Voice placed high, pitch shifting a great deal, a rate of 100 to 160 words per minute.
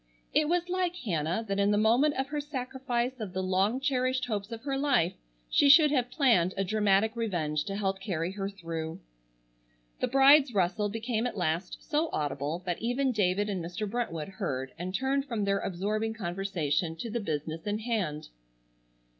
No: high, 210 Hz; wide, 6.0 semitones; average, 180 wpm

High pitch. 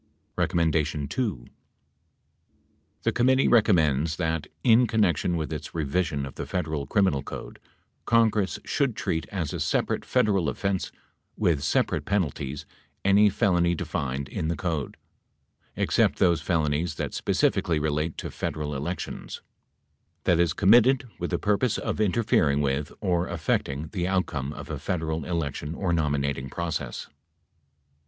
No: very low, 80 Hz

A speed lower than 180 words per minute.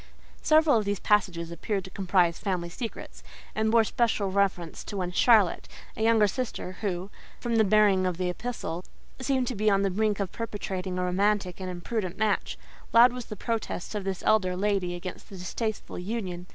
No: average, 185 wpm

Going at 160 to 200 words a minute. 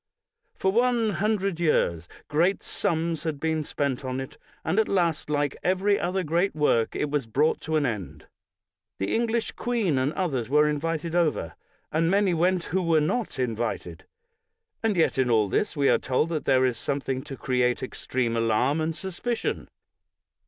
Yes: average, 170 wpm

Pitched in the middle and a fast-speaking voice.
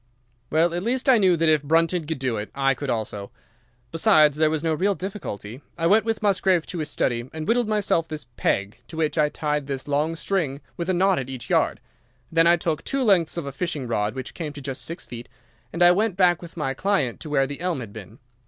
Yes: medium, 160 Hz; fast, 235 wpm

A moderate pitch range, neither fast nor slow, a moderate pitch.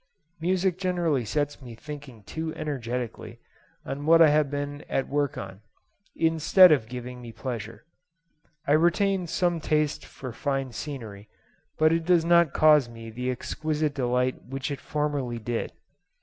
Yes: average, 4.2 semitones; average, 150 wpm; medium, 145 Hz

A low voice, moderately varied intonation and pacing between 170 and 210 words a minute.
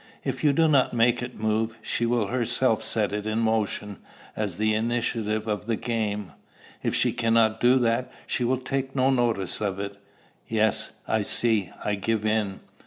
No: low, 110 Hz; narrow, 2.3 semitones; average, 175 wpm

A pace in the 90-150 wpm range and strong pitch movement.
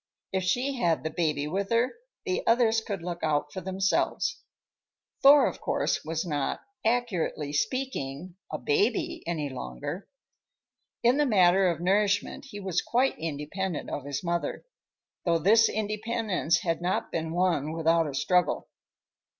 Yes: average, 145 wpm; wide, 5.8 semitones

